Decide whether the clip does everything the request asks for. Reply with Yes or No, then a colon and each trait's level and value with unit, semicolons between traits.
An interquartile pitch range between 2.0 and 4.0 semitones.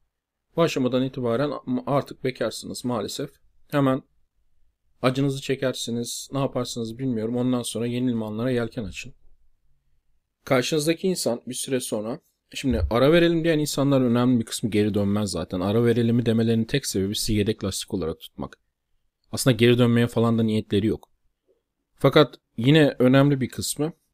Yes: average, 3.5 semitones